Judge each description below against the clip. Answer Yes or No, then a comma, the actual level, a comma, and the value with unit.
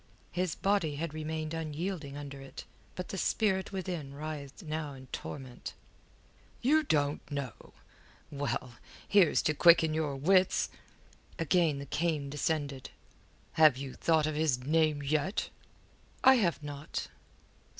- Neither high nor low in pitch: Yes, medium, 155 Hz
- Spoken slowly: Yes, slow, 130 wpm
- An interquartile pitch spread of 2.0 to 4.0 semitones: Yes, average, 3.2 semitones